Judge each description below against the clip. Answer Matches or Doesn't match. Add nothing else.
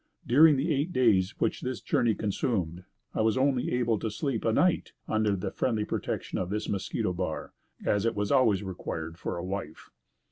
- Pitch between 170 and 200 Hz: Doesn't match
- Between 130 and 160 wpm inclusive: Doesn't match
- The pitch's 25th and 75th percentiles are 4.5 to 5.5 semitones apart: Matches